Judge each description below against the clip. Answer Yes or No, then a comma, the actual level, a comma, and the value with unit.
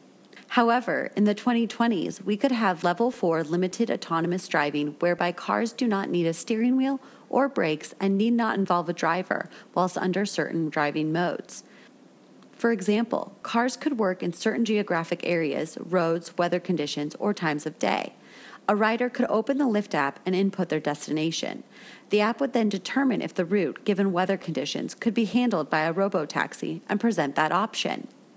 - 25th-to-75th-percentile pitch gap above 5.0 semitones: Yes, wide, 5.6 semitones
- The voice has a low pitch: No, high, 195 Hz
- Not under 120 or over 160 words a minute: No, average, 175 wpm